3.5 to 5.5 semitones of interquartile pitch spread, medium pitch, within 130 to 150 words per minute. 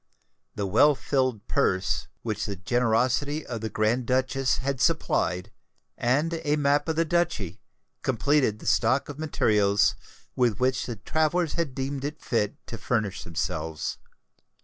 No: average, 5.2 semitones; low, 130 Hz; average, 145 wpm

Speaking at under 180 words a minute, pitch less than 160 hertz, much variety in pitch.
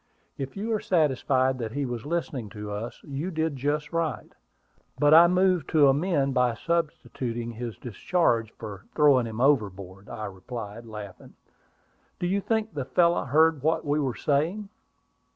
Yes: average, 155 wpm; medium, 140 Hz; wide, 5.9 semitones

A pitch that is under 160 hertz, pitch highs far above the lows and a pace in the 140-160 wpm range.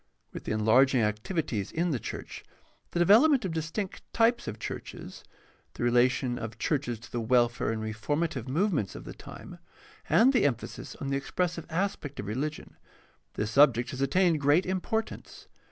No: medium, 140 Hz; wide, 6.6 semitones; average, 170 wpm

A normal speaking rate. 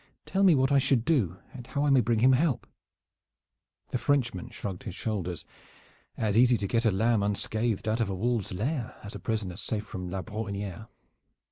Yes: average, 195 wpm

